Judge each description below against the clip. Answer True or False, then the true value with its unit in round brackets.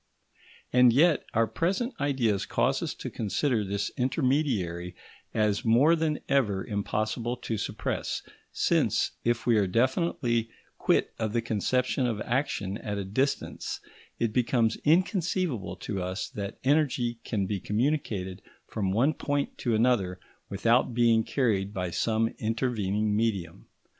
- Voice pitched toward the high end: False (115 Hz)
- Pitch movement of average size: True (4.3 semitones)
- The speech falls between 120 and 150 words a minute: True (135 wpm)